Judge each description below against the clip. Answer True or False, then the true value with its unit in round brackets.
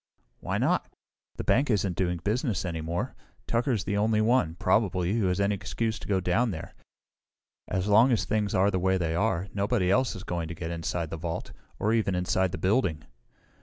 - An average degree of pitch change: True (3.8 semitones)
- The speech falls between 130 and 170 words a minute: False (205 wpm)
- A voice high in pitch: False (95 Hz)